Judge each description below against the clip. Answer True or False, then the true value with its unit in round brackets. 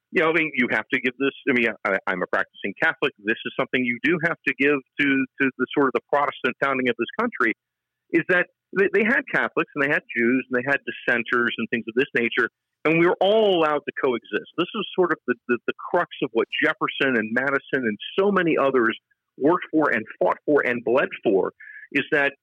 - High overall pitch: False (140 Hz)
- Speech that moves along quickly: True (235 wpm)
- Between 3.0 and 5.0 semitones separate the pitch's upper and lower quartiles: True (4.7 semitones)